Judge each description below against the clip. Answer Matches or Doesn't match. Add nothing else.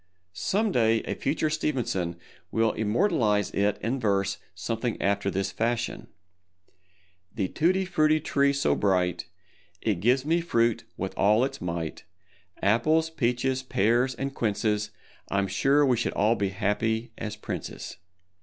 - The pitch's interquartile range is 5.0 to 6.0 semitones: Matches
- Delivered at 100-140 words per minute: Matches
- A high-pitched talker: Doesn't match